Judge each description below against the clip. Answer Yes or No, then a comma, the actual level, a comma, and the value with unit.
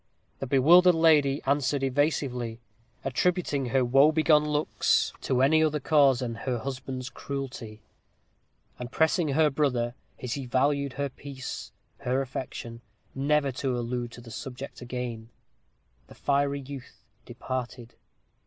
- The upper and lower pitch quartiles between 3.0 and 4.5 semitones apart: No, narrow, 2.6 semitones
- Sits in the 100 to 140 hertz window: Yes, low, 135 Hz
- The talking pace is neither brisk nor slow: No, slow, 130 wpm